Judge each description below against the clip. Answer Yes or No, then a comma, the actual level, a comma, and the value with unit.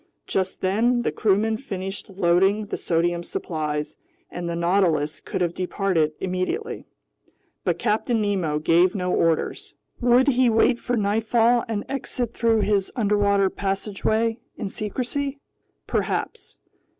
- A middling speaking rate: No, slow, 125 wpm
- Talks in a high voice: Yes, high, 200 Hz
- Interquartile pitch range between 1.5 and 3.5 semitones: No, average, 4.1 semitones